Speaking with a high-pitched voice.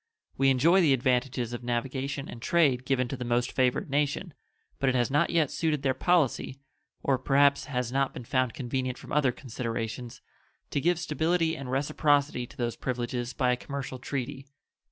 No: low, 135 Hz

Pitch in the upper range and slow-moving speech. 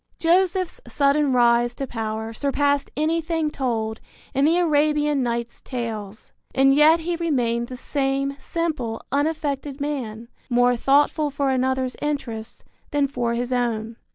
Yes: very high, 270 Hz; slow, 130 wpm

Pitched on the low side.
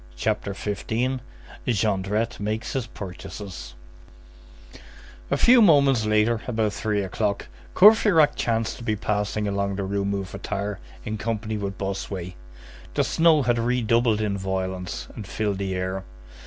Yes: low, 105 Hz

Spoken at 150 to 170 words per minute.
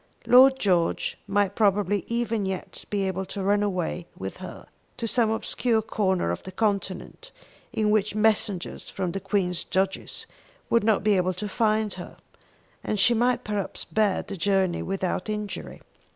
Yes: average, 160 wpm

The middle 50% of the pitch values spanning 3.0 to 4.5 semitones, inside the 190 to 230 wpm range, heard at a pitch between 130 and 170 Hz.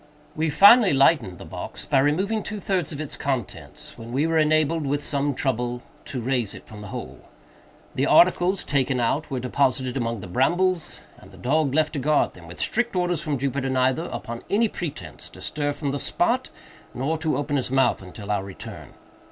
Yes: average, 4.1 semitones; average, 195 wpm; medium, 140 Hz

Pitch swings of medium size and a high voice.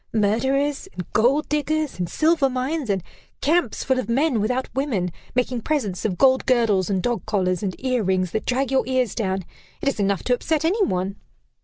No: wide, 5.7 semitones; very high, 250 Hz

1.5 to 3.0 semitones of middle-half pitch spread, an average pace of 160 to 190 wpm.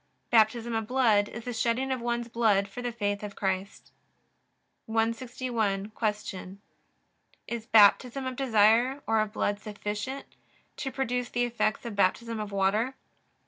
No: average, 2.7 semitones; average, 145 wpm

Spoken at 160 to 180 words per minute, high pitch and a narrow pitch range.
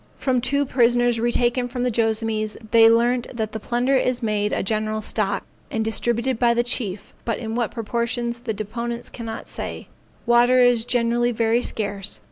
Yes: average, 170 wpm; high, 235 Hz; narrow, 1.7 semitones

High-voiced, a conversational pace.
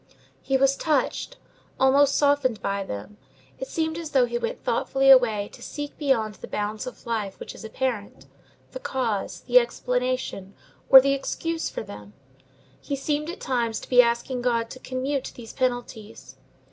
Yes: very high, 255 Hz; average, 165 wpm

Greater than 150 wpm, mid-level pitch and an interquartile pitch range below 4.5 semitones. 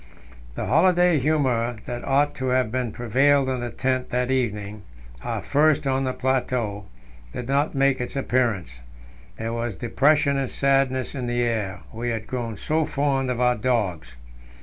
No: average, 160 wpm; low, 125 Hz; average, 2.8 semitones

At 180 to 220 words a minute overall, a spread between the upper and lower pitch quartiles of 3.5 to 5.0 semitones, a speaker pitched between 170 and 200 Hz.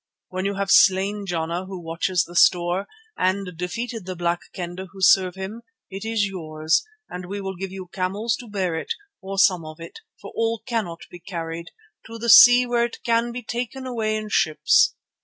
Yes: average, 195 wpm; average, 3.9 semitones; high, 190 Hz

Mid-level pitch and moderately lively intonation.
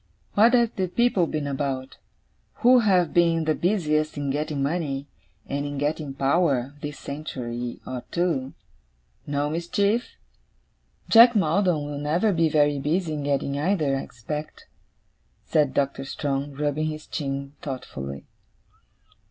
Yes: medium, 150 Hz; average, 3.7 semitones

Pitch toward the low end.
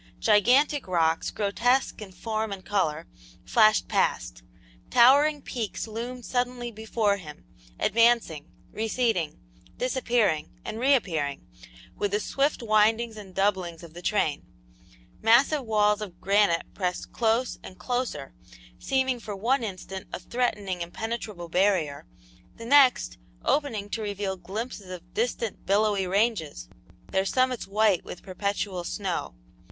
No: high, 210 Hz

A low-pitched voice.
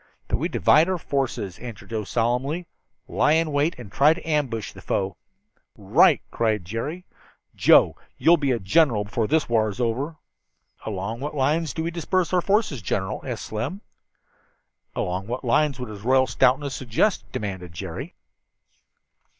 Yes: low, 125 Hz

